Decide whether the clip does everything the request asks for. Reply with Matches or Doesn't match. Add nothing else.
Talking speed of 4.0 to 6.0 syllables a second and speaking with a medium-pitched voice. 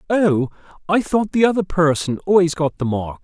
Matches